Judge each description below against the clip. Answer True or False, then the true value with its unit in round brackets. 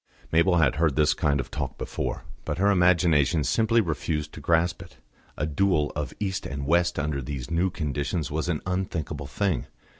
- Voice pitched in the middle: False (80 Hz)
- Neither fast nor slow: True (180 wpm)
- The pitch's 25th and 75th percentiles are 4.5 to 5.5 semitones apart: False (3.4 semitones)